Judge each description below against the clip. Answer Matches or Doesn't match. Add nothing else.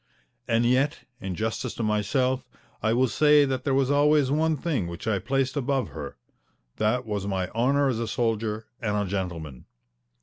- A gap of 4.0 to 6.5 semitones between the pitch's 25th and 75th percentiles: Matches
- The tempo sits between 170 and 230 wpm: Matches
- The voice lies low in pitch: Matches